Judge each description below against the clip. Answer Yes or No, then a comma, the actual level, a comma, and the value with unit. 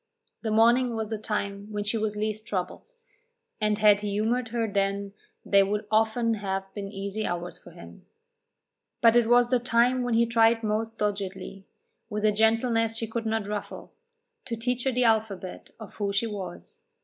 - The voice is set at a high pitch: Yes, high, 215 Hz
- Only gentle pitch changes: Yes, narrow, 2.2 semitones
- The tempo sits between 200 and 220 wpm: No, average, 180 wpm